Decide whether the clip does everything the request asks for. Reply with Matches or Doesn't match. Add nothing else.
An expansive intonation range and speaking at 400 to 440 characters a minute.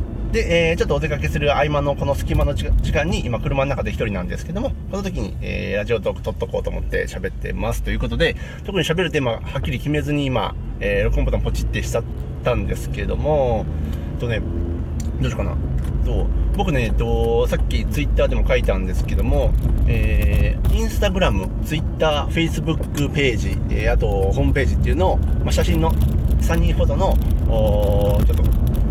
Matches